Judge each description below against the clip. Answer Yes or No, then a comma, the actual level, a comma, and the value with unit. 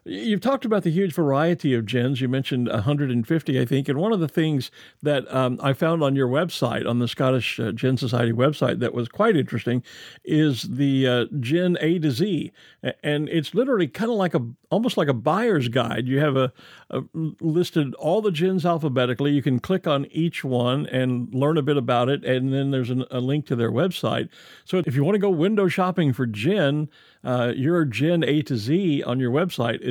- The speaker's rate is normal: No, fast, 210 wpm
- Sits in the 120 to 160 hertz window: Yes, medium, 140 Hz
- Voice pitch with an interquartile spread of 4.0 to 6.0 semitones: Yes, average, 4.6 semitones